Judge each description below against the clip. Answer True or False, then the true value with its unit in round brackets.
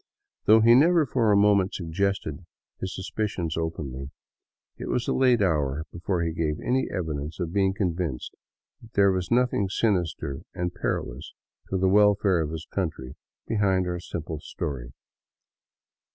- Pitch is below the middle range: True (90 Hz)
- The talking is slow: False (150 wpm)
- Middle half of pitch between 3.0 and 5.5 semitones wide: True (4.2 semitones)